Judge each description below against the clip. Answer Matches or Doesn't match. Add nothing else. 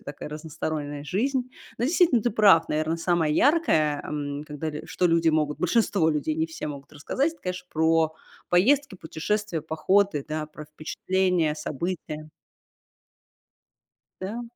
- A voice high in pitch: Doesn't match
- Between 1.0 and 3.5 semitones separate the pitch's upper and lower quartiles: Doesn't match